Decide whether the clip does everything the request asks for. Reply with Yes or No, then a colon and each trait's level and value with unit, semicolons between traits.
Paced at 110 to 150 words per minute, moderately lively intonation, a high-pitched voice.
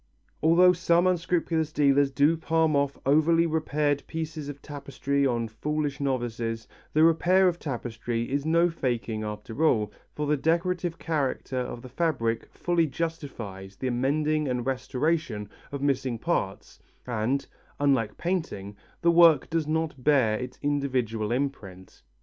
No: average, 140 wpm; average, 4.9 semitones; medium, 140 Hz